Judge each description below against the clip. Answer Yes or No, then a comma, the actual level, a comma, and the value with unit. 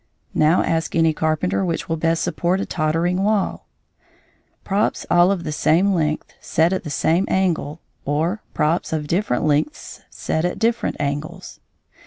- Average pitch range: Yes, average, 3.2 semitones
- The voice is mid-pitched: Yes, medium, 165 Hz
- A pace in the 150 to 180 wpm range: Yes, average, 155 wpm